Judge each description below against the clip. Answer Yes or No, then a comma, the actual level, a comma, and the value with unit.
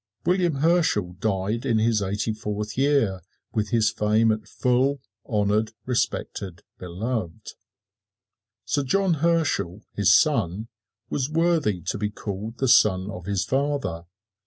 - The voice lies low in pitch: Yes, low, 110 Hz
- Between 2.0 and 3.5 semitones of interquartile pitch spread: No, average, 5.3 semitones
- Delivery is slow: Yes, slow, 130 wpm